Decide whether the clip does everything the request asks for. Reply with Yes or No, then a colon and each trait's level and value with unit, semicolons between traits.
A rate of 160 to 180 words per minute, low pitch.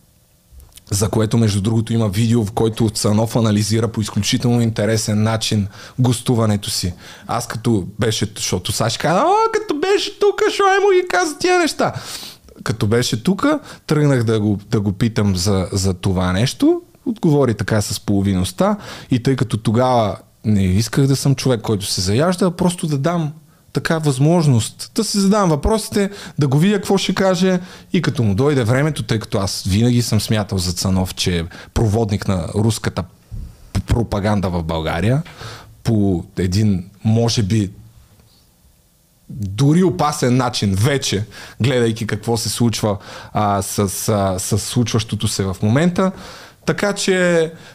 No: average, 150 wpm; low, 115 Hz